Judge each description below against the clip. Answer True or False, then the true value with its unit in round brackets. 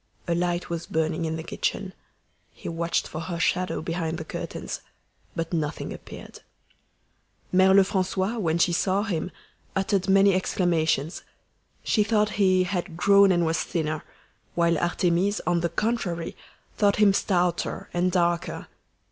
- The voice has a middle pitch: True (175 Hz)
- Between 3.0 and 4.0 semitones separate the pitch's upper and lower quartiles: False (2.5 semitones)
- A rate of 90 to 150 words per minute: True (140 wpm)